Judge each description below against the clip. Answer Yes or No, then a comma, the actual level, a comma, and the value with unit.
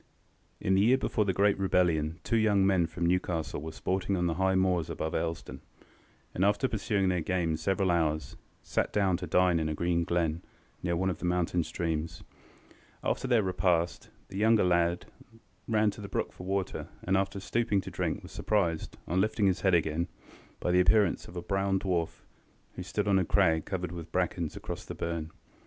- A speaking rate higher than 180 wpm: Yes, average, 195 wpm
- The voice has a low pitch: Yes, very low, 90 Hz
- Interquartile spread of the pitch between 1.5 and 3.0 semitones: Yes, narrow, 2.5 semitones